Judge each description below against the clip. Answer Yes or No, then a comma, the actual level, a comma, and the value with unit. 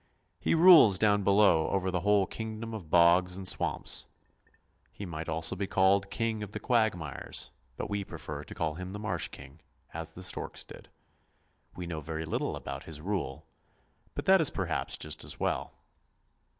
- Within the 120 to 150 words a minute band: No, average, 175 wpm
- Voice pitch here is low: Yes, very low, 95 Hz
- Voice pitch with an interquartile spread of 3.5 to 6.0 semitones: Yes, average, 4.1 semitones